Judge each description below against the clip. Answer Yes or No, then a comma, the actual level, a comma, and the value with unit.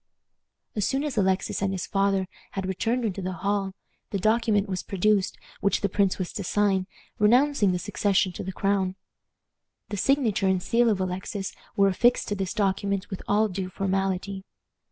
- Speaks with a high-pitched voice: Yes, high, 195 Hz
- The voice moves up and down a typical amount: No, narrow, 1.7 semitones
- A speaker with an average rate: Yes, average, 175 wpm